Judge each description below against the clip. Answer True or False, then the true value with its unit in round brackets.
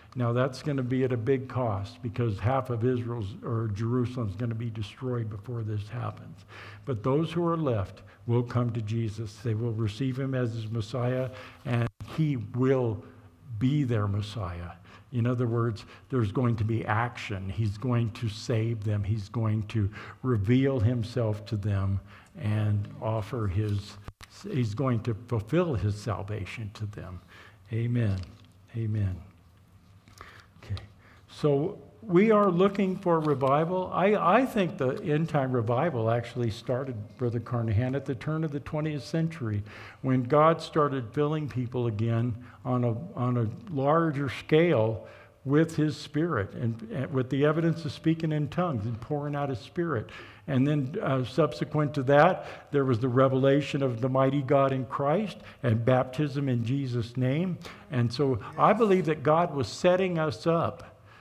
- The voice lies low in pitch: True (120 Hz)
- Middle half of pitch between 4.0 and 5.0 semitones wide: True (4.7 semitones)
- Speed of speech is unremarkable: True (160 wpm)